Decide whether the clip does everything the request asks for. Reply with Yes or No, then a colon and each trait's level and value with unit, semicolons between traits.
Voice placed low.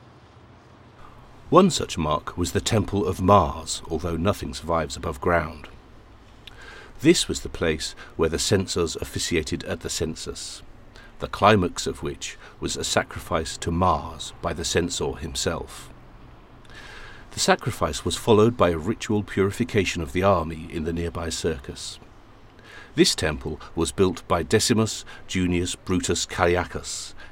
Yes: very low, 90 Hz